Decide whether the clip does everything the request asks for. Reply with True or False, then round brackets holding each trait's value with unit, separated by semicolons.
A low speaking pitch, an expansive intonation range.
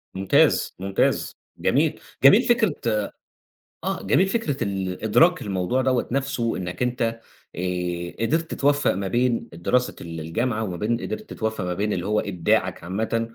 True (110 Hz; 6.1 semitones)